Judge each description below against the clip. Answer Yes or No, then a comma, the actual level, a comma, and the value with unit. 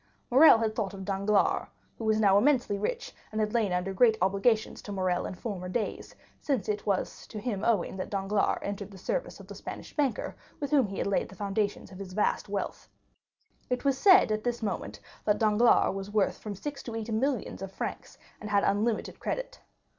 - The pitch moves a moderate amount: Yes, average, 3.3 semitones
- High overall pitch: Yes, high, 210 Hz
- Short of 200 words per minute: No, fast, 205 wpm